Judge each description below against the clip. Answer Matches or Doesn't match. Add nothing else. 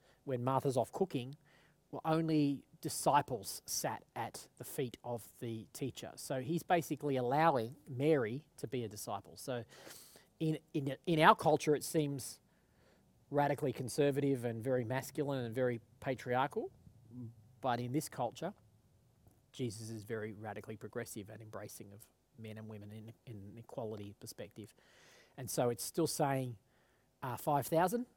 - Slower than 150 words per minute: Matches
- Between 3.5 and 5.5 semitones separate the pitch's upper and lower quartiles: Matches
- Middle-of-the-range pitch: Doesn't match